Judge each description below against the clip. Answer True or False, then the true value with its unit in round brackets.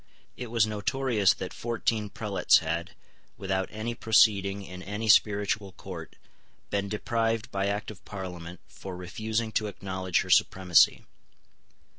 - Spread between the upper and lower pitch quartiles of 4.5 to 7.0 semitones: False (2.6 semitones)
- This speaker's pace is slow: True (130 wpm)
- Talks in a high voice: False (100 Hz)